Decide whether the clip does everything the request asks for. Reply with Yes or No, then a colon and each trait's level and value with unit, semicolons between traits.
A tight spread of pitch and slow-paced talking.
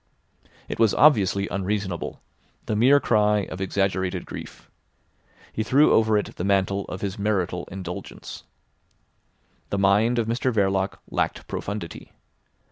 Yes: narrow, 2.3 semitones; slow, 125 wpm